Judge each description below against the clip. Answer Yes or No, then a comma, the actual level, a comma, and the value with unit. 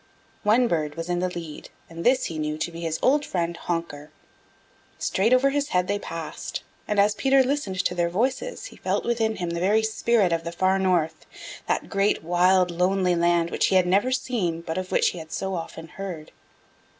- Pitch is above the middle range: No, medium, 180 Hz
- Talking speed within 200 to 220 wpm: Yes, fast, 205 wpm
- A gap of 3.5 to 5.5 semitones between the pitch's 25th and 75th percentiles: Yes, average, 4.2 semitones